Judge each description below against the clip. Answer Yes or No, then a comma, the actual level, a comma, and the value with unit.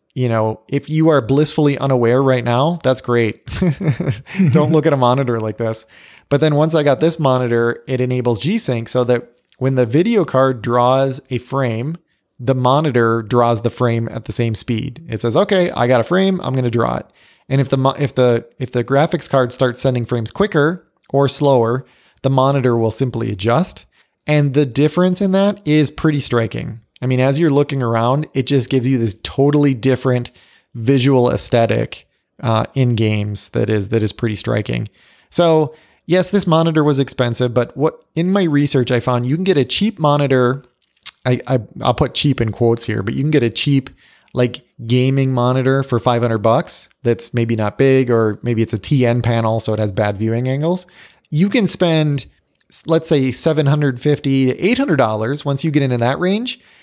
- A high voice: No, low, 130 Hz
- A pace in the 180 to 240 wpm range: Yes, average, 190 wpm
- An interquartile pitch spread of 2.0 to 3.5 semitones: No, average, 3.9 semitones